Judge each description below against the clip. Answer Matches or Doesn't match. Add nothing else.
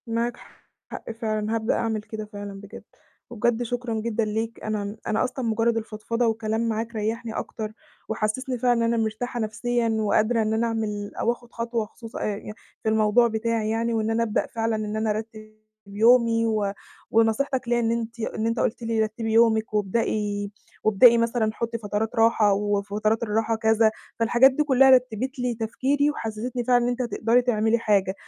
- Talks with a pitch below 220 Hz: Doesn't match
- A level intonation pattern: Matches